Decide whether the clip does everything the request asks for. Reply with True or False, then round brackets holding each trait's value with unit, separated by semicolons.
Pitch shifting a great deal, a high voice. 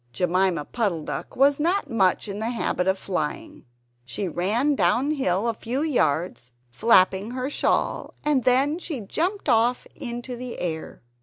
True (6.3 semitones; 230 Hz)